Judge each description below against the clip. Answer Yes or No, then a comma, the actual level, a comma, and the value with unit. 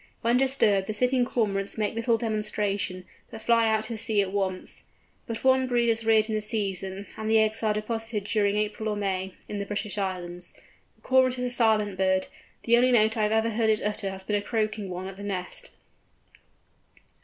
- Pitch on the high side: Yes, high, 215 Hz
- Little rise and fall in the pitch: Yes, narrow, 2.3 semitones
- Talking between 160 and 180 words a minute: No, fast, 205 wpm